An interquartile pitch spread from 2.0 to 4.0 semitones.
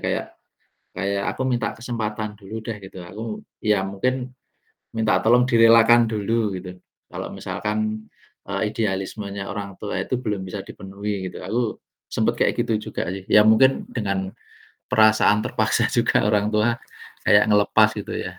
Yes: narrow, 2.5 semitones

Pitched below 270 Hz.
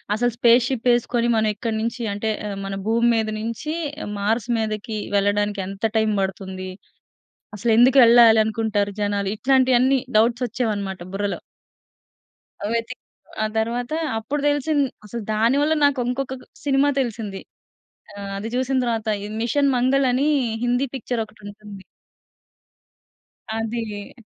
Yes: high, 230 Hz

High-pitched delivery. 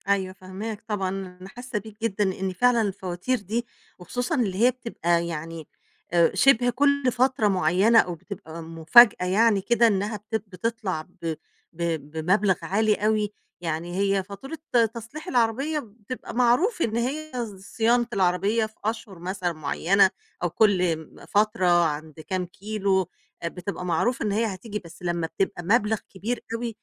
Yes: high, 200 Hz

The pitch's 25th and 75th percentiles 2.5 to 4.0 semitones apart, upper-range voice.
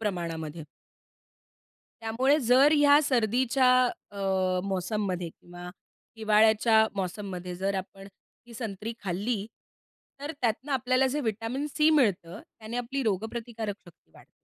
No: average, 4.7 semitones; high, 220 Hz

